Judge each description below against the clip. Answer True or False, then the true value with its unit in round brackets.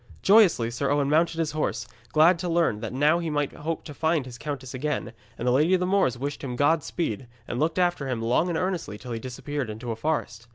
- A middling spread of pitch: True (4.8 semitones)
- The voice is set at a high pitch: False (145 Hz)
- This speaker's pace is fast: True (235 wpm)